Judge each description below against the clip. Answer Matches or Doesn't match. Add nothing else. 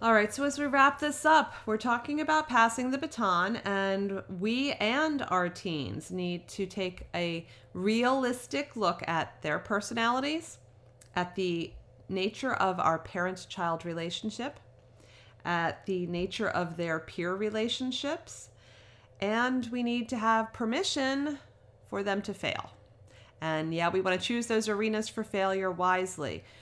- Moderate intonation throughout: Doesn't match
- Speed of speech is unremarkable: Matches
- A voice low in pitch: Doesn't match